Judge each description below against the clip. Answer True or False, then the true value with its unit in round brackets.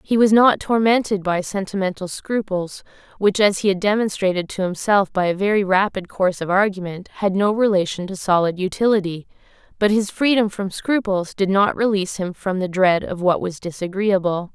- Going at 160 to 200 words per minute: True (175 wpm)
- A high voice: True (195 Hz)